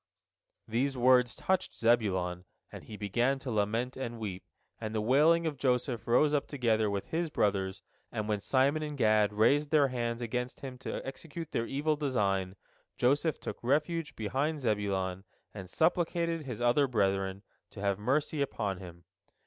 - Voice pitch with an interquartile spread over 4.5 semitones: Yes, wide, 5.6 semitones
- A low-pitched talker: Yes, low, 120 Hz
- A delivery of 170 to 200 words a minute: No, average, 160 wpm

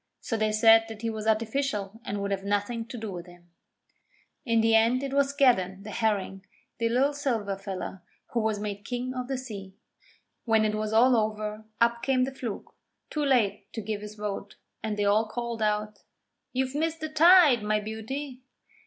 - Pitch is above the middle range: Yes, high, 220 Hz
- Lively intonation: No, average, 3.3 semitones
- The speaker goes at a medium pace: Yes, average, 190 wpm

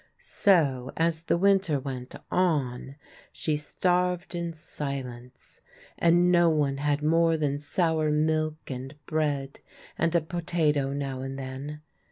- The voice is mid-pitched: Yes, medium, 150 Hz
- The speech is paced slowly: Yes, slow, 130 wpm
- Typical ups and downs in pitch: Yes, average, 3.5 semitones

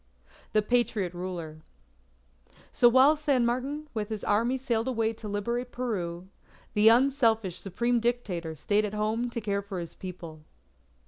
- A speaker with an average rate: Yes, average, 145 wpm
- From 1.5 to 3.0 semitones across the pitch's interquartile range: No, average, 4.0 semitones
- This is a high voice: Yes, high, 220 Hz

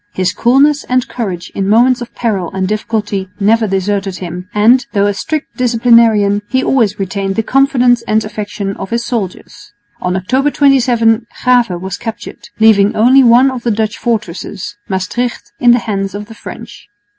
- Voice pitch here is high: Yes, high, 220 Hz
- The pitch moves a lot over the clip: No, average, 3.6 semitones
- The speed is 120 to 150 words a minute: No, average, 170 wpm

